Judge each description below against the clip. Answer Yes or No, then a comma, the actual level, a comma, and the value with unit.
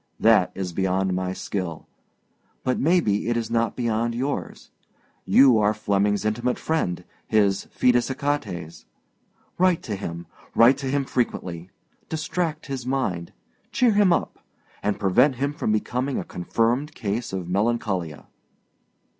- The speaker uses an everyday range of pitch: No, wide, 5.7 semitones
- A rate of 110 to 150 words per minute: Yes, slow, 135 wpm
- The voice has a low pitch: Yes, low, 115 Hz